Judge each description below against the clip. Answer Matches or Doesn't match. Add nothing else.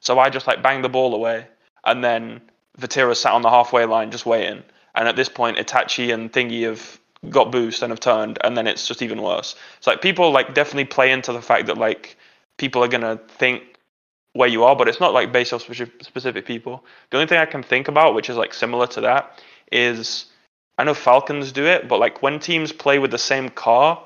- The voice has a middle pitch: Doesn't match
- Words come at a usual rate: Doesn't match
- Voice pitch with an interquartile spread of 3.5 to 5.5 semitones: Doesn't match